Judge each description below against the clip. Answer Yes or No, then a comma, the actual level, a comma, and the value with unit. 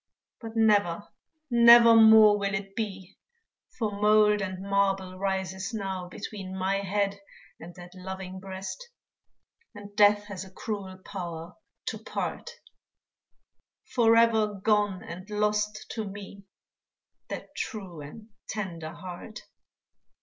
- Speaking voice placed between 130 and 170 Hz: No, high, 200 Hz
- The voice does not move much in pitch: Yes, narrow, 2.0 semitones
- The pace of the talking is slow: Yes, slow, 115 wpm